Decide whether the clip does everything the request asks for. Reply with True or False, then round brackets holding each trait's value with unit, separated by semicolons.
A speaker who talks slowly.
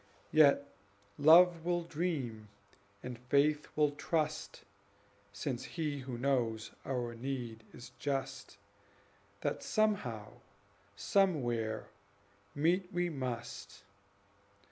True (90 wpm)